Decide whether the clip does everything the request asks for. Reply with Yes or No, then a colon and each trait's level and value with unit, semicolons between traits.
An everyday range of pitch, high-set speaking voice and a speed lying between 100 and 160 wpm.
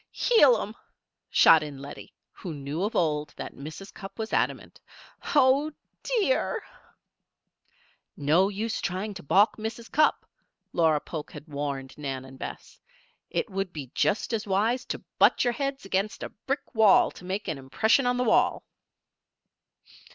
No: wide, 7.3 semitones; high, 195 Hz; average, 150 wpm